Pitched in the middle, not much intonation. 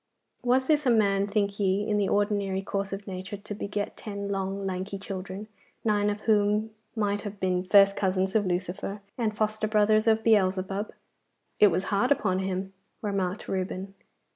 No: high, 200 Hz; narrow, 1.7 semitones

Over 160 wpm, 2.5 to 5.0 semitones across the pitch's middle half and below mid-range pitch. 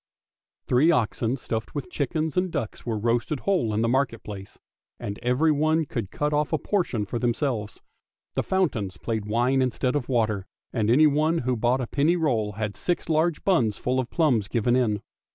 No: average, 180 wpm; wide, 5.5 semitones; low, 125 Hz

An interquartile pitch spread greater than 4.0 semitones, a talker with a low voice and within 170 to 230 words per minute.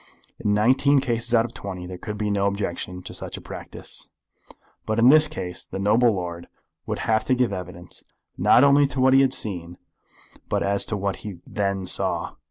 Yes: average, 4.7 semitones; low, 105 Hz; average, 200 wpm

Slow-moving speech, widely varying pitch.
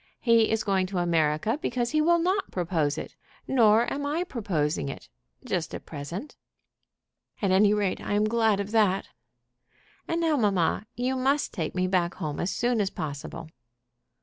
No: average, 170 wpm; wide, 5.8 semitones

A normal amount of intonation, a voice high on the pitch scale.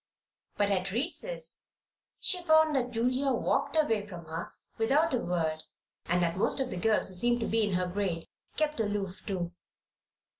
No: wide, 6.6 semitones; high, 215 Hz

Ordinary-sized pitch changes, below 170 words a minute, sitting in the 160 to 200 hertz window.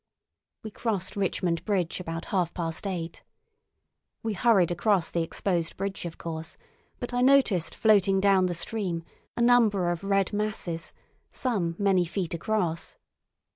Yes: average, 3.7 semitones; average, 140 wpm; high, 190 Hz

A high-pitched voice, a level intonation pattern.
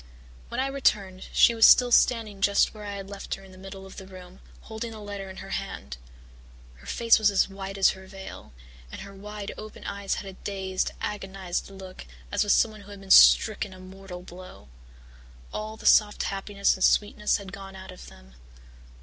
Yes: high, 195 Hz; narrow, 1.6 semitones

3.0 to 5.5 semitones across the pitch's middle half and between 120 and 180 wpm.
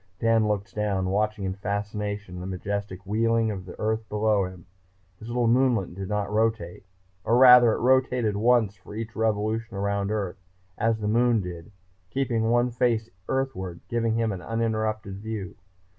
No: narrow, 2.4 semitones; average, 160 wpm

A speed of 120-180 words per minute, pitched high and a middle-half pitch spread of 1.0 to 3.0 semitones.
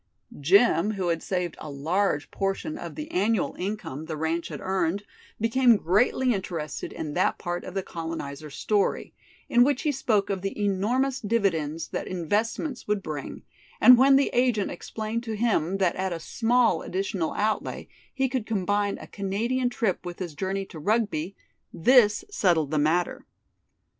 No: average, 165 wpm; high, 195 Hz; average, 5.1 semitones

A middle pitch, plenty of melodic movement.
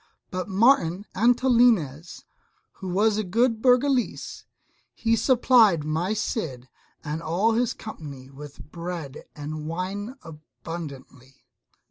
Yes: medium, 180 Hz; wide, 6.8 semitones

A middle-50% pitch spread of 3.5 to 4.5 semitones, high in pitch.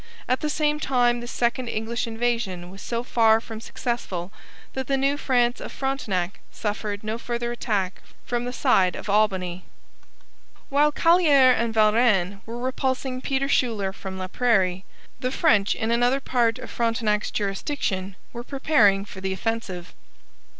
Yes: average, 4.2 semitones; high, 235 Hz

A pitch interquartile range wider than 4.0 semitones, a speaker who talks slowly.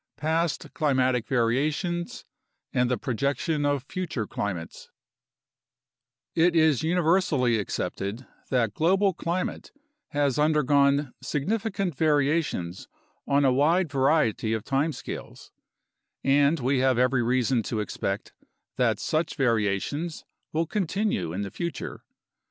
Yes: average, 4.8 semitones; slow, 115 wpm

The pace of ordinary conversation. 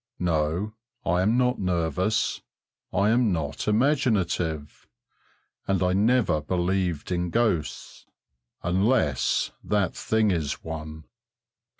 No: slow, 100 wpm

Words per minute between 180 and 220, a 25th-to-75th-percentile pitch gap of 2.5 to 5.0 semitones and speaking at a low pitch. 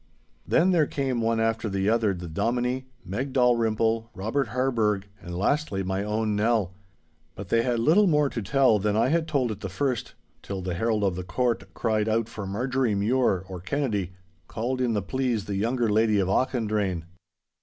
Yes: average, 185 wpm; average, 4.1 semitones; low, 110 Hz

